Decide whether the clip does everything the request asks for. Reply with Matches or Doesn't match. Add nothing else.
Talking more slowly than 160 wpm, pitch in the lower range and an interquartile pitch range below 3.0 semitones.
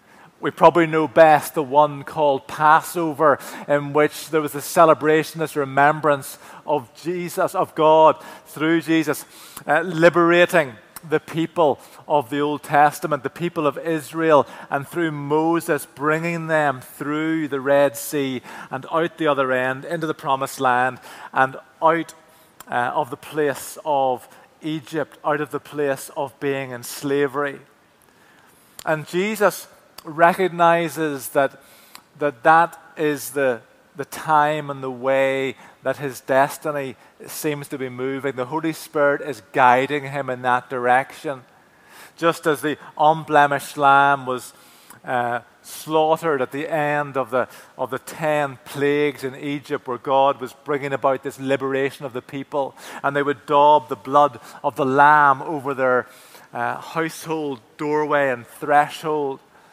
Doesn't match